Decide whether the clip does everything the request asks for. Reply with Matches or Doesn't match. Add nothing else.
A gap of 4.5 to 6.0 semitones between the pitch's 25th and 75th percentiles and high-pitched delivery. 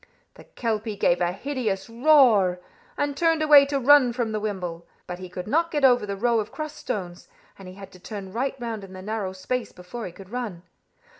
Matches